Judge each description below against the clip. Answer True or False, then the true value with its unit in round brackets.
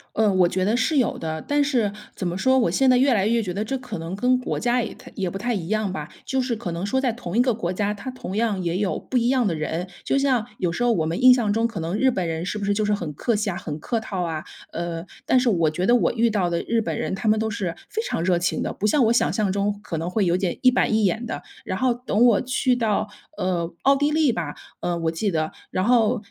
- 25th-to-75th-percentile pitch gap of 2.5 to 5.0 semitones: False (5.4 semitones)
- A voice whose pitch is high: True (210 Hz)